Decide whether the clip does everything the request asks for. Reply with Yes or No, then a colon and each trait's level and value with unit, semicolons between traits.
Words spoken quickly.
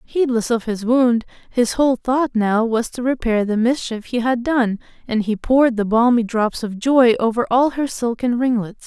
No: average, 195 wpm